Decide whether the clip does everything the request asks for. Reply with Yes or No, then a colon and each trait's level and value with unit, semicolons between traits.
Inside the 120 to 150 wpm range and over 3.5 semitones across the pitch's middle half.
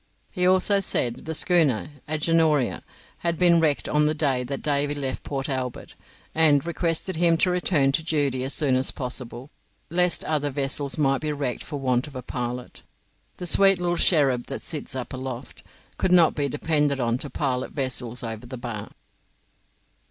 No: average, 175 wpm; average, 3.9 semitones